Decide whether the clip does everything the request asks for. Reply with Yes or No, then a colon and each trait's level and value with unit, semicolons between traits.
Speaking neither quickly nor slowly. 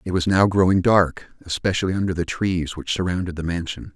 Yes: average, 195 wpm